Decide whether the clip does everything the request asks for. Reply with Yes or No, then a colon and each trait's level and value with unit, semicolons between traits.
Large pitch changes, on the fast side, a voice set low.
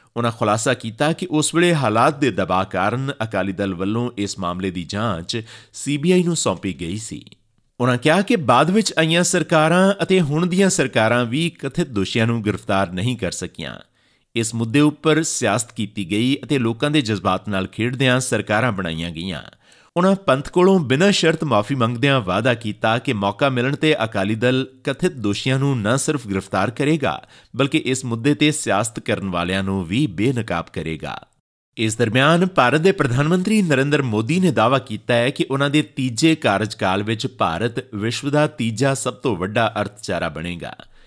Yes: wide, 6.3 semitones; fast, 170 wpm; low, 125 Hz